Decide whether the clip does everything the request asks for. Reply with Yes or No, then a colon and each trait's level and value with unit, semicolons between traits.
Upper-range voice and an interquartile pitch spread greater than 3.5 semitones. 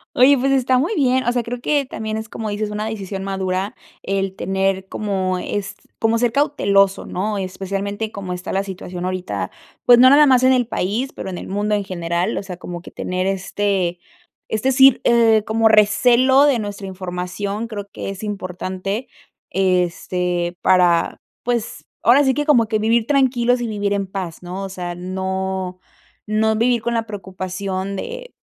Yes: high, 205 Hz; average, 4.0 semitones